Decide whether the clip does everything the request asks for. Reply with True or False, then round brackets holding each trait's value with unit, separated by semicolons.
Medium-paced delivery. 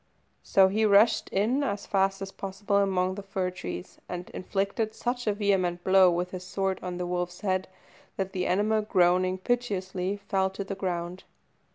True (175 wpm)